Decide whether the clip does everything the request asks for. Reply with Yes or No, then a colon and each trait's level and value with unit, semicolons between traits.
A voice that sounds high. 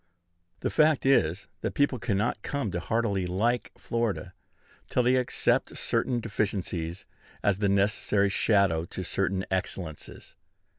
No: low, 100 Hz